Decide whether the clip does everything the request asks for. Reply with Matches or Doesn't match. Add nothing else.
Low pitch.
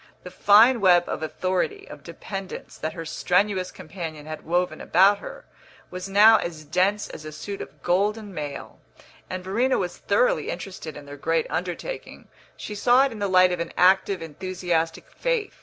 Doesn't match